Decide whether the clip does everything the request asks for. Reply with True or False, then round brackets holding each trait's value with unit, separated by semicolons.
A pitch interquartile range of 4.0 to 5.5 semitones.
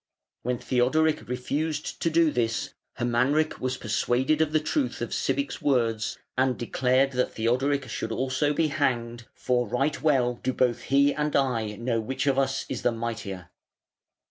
False (3.4 semitones)